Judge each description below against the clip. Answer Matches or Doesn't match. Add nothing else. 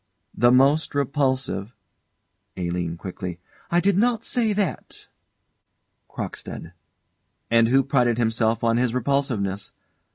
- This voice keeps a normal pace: Doesn't match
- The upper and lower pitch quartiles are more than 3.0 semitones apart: Matches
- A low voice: Matches